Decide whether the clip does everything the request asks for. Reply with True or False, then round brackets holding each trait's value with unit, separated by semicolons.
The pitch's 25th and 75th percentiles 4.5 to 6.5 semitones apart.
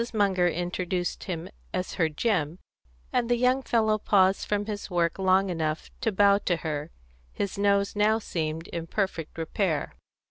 False (3.6 semitones)